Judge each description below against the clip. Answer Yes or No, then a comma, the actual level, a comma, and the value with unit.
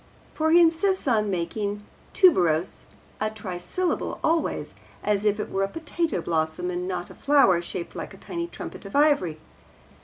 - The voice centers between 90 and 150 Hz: No, high, 210 Hz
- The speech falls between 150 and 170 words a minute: Yes, average, 160 wpm